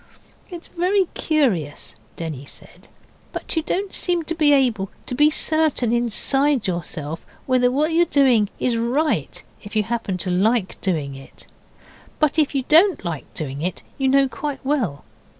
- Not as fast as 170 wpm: Yes, average, 160 wpm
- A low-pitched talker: No, very high, 250 Hz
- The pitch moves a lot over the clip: Yes, wide, 8.3 semitones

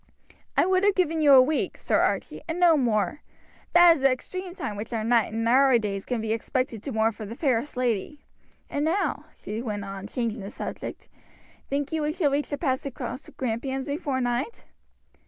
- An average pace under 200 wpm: No, fast, 205 wpm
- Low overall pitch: No, very high, 260 Hz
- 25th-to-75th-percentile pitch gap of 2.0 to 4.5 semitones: No, average, 4.9 semitones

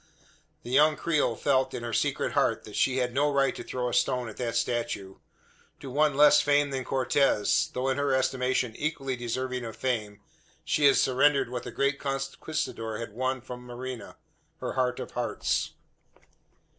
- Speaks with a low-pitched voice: Yes, low, 130 Hz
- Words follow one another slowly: No, average, 175 wpm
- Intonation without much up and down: Yes, narrow, 2.2 semitones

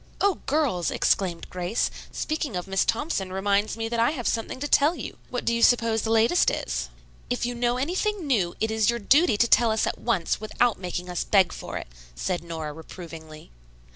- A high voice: Yes, high, 220 Hz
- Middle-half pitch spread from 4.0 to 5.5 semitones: Yes, average, 5.2 semitones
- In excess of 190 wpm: Yes, average, 200 wpm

